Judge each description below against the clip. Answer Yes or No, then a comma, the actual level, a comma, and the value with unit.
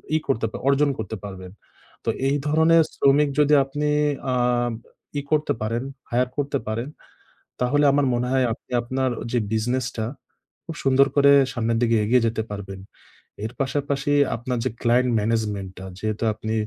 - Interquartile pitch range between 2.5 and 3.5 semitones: No, average, 3.9 semitones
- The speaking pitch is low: Yes, low, 125 Hz